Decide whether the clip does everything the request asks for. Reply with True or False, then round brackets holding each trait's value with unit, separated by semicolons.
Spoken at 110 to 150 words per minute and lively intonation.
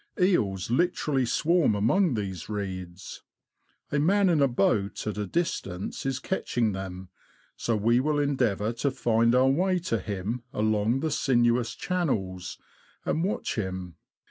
True (145 wpm; 6.5 semitones)